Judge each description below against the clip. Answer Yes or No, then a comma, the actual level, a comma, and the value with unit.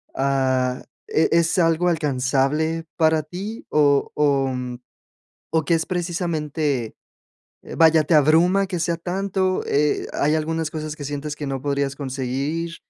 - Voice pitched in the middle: Yes, medium, 155 Hz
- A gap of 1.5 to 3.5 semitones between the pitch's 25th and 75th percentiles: Yes, average, 3.1 semitones